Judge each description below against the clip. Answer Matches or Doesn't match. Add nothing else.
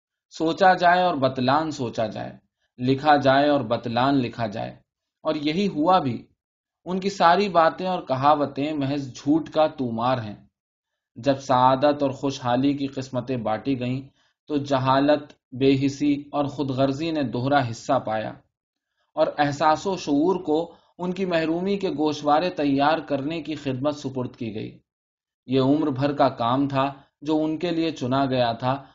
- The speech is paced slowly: Doesn't match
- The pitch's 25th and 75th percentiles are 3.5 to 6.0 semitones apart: Doesn't match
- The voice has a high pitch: Doesn't match